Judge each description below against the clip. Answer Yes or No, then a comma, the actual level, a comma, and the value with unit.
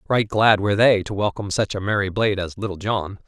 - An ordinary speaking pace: No, fast, 240 wpm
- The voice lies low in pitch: Yes, low, 100 Hz